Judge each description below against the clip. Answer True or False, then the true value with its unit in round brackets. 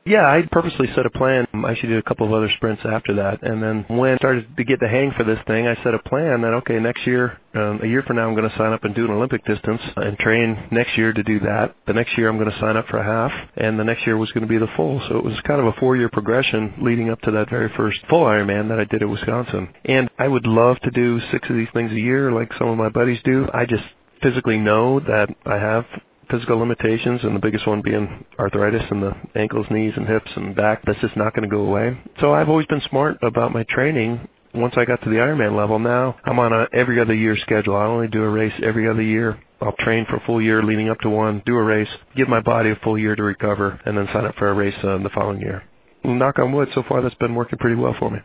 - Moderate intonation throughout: False (2.3 semitones)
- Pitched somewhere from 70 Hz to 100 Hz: False (115 Hz)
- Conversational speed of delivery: False (280 wpm)